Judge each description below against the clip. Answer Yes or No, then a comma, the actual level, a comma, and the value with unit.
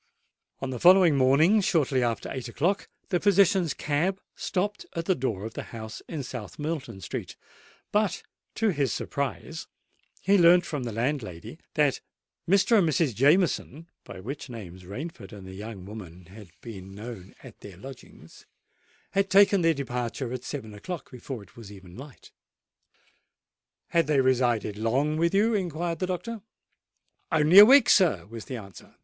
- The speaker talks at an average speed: Yes, average, 160 wpm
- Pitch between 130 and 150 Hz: Yes, low, 135 Hz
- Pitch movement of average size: No, wide, 7.8 semitones